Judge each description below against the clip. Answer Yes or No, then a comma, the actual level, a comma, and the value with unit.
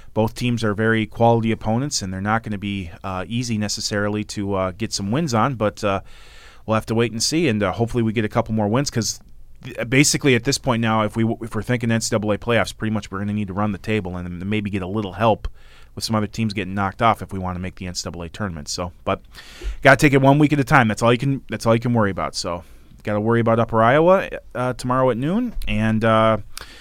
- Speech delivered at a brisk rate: Yes, fast, 265 wpm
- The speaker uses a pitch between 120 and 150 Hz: No, low, 110 Hz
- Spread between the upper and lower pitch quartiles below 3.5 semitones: Yes, narrow, 2.4 semitones